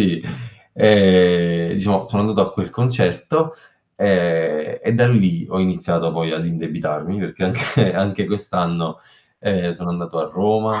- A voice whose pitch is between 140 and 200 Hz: No, very low, 90 Hz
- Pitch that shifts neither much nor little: Yes, average, 3.3 semitones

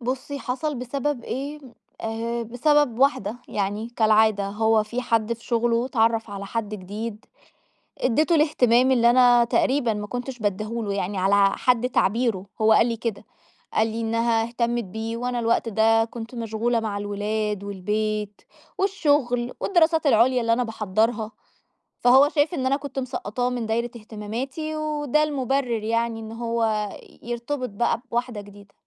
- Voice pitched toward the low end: No, high, 230 Hz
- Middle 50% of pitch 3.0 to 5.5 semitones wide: No, narrow, 2.6 semitones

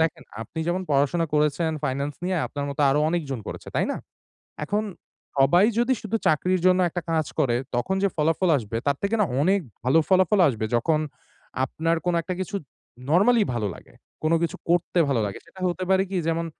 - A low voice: No, medium, 165 Hz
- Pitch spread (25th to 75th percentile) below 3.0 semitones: No, average, 4.7 semitones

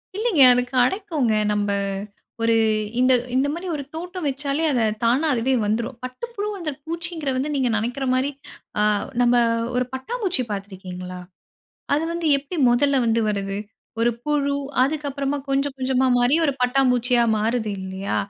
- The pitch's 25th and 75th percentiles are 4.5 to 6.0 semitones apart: No, average, 4.0 semitones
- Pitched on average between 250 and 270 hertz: Yes, very high, 265 Hz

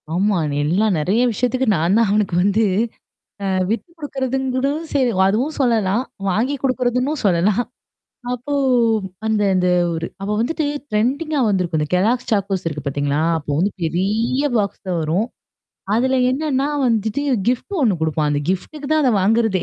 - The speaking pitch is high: Yes, high, 215 Hz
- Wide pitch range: Yes, wide, 5.7 semitones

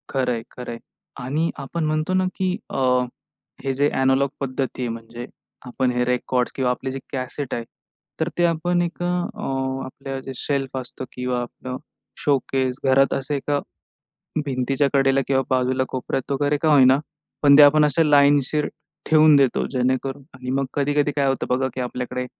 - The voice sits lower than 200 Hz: Yes, low, 135 Hz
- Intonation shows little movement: Yes, narrow, 2.2 semitones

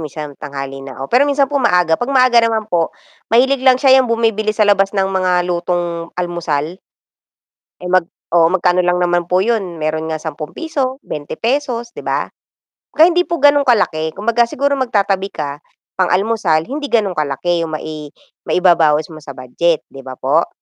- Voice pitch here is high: No, medium, 180 Hz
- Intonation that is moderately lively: No, wide, 6.9 semitones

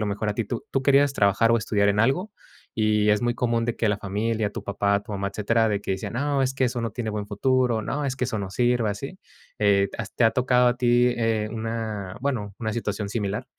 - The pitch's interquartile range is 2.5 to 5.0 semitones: Yes, average, 3.0 semitones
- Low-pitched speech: Yes, low, 115 Hz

